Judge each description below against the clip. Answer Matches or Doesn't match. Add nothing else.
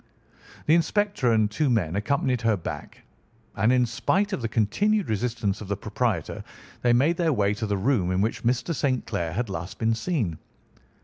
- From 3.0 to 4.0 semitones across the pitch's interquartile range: Doesn't match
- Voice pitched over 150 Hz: Doesn't match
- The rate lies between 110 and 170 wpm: Doesn't match